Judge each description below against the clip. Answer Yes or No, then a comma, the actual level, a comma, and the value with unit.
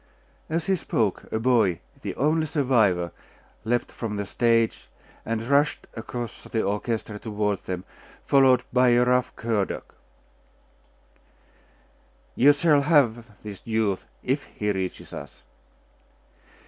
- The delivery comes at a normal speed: No, slow, 120 wpm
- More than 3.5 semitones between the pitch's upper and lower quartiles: Yes, average, 4.1 semitones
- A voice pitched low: Yes, low, 115 Hz